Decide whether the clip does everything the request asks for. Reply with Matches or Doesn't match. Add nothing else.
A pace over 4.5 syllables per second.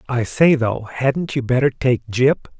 Doesn't match